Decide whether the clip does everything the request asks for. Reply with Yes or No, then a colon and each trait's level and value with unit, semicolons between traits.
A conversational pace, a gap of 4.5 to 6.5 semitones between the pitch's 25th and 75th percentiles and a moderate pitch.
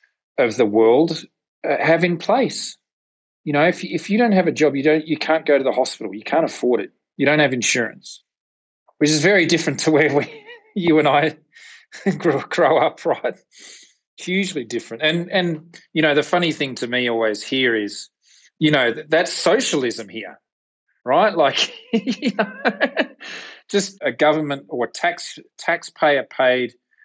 Yes: average, 175 wpm; average, 5.1 semitones; medium, 160 Hz